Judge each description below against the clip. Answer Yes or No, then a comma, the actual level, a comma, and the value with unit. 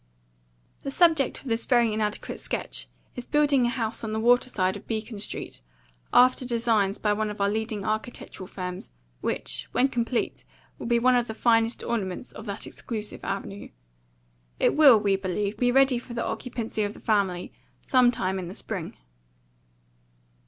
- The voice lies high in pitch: Yes, high, 225 Hz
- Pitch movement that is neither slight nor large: Yes, average, 3.2 semitones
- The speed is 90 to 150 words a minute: No, average, 165 wpm